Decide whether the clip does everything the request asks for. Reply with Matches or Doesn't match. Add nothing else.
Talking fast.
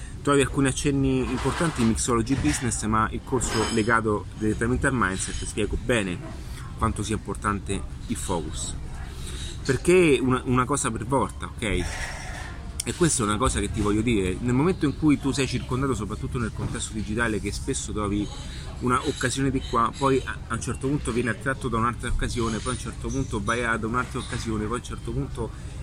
Matches